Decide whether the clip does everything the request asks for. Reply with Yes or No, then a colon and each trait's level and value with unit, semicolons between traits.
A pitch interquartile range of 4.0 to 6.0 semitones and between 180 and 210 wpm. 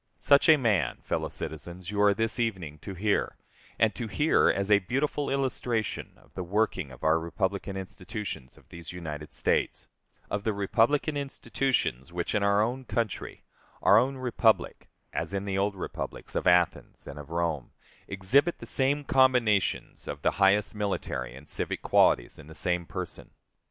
No: average, 5.1 semitones; average, 165 wpm